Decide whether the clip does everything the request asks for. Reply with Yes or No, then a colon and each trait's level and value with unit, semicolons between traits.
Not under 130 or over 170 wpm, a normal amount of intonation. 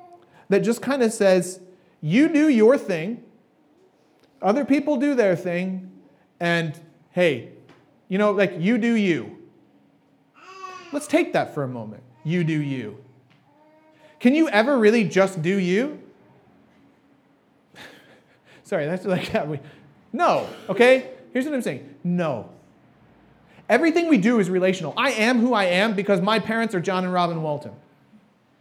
No: average, 145 wpm; wide, 6.4 semitones